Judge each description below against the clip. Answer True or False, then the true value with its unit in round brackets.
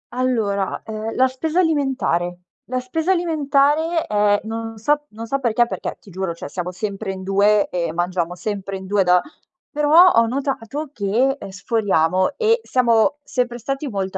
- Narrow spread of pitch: False (6.1 semitones)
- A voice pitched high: True (225 Hz)